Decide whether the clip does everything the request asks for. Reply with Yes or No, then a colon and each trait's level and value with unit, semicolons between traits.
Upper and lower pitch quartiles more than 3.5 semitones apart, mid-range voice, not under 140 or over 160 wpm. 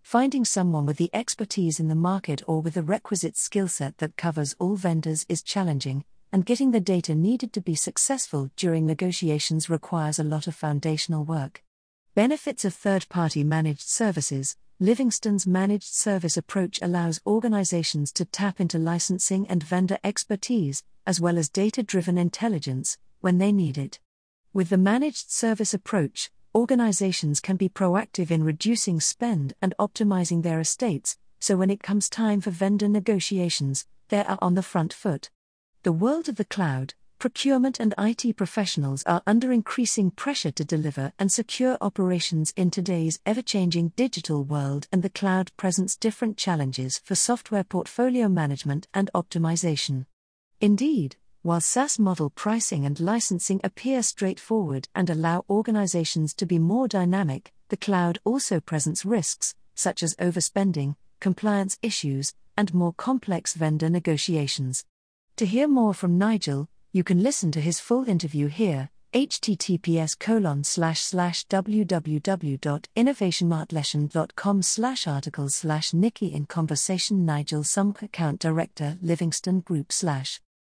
Yes: average, 4.6 semitones; medium, 180 Hz; average, 145 wpm